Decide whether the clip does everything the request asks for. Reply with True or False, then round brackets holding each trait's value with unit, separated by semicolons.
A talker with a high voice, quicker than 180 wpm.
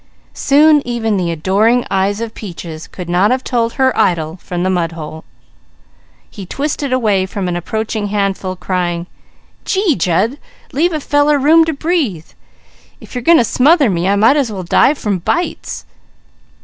False (210 Hz; 165 wpm)